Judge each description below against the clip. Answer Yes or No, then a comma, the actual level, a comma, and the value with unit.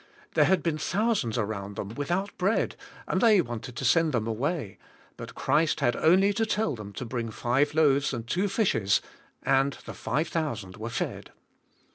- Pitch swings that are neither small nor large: No, wide, 7.5 semitones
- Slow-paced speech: No, average, 175 wpm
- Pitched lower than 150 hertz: Yes, medium, 140 Hz